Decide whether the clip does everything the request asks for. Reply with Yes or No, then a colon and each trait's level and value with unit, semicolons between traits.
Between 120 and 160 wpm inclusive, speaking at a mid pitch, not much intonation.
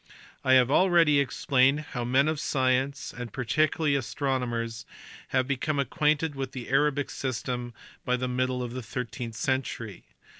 No: average, 145 wpm; low, 130 Hz; narrow, 2.3 semitones